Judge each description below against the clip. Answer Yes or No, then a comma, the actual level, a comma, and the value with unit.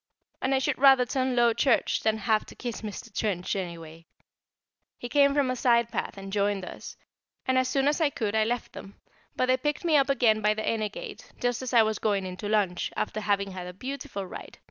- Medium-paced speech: No, fast, 230 wpm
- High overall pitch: Yes, high, 225 Hz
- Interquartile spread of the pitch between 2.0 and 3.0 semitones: No, average, 4.3 semitones